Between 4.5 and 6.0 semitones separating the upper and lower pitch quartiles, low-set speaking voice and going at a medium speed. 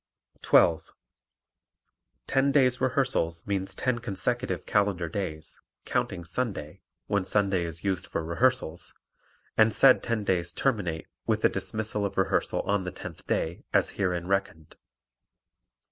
No: average, 5.1 semitones; low, 100 Hz; slow, 130 wpm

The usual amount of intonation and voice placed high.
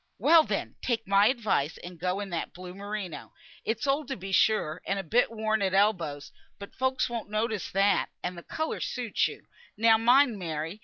Yes: average, 4.1 semitones; high, 205 Hz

